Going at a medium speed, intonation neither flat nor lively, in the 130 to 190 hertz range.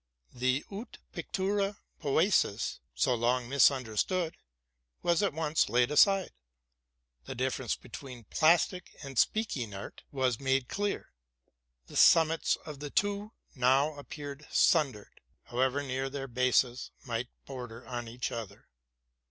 No: slow, 125 wpm; average, 4.6 semitones; low, 135 Hz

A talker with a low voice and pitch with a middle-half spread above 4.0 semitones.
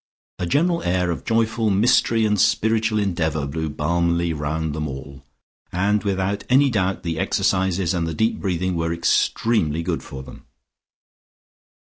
Yes: very low, 90 Hz; average, 4.5 semitones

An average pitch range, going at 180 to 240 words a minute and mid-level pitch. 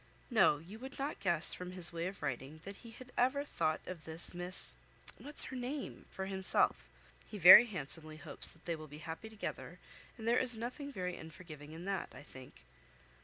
No: wide, 6.4 semitones; average, 190 wpm; medium, 180 Hz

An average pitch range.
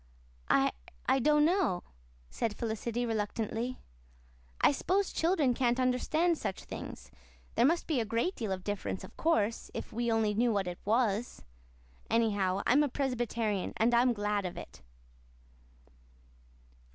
Yes: average, 4.0 semitones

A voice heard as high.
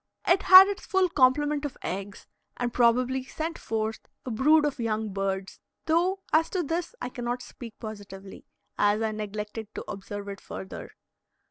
Yes: high, 240 Hz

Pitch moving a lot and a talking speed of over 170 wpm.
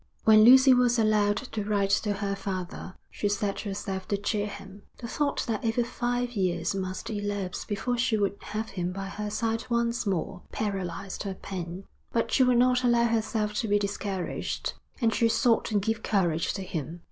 No: average, 2.9 semitones; average, 185 wpm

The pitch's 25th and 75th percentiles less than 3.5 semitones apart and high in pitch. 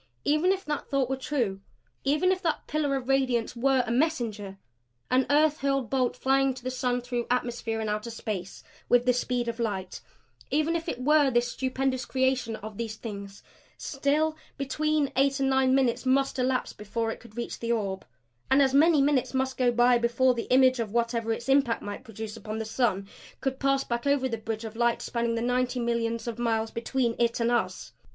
Yes: average, 2.8 semitones; very high, 250 Hz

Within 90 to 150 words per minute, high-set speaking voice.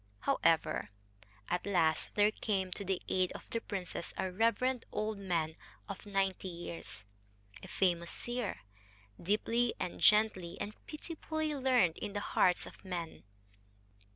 Yes: slow, 135 wpm; high, 195 Hz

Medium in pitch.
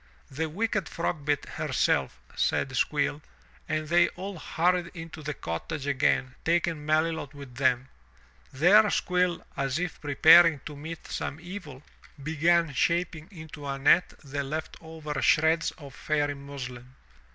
Yes: medium, 155 Hz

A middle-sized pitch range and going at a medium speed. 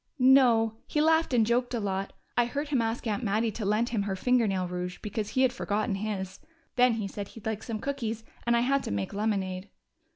No: average, 3.5 semitones; fast, 225 wpm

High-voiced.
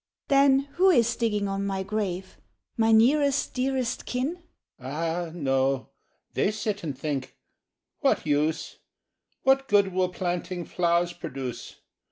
Yes: high, 195 Hz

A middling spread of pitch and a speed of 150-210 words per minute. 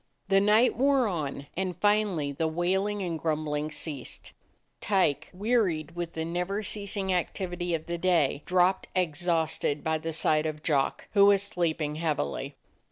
Yes: average, 3.8 semitones; average, 155 wpm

